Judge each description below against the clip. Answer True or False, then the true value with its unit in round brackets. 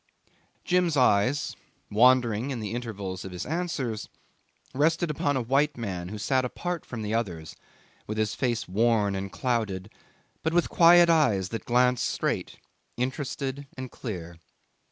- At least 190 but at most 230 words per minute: False (145 wpm)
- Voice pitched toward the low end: True (120 Hz)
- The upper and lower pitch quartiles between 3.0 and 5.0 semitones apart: False (5.4 semitones)